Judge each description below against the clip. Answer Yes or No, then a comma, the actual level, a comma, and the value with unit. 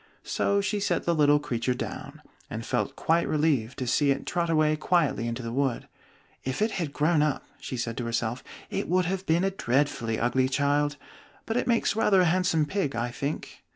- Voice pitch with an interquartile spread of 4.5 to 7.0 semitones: Yes, wide, 5.5 semitones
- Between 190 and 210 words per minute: Yes, average, 200 wpm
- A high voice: No, medium, 150 Hz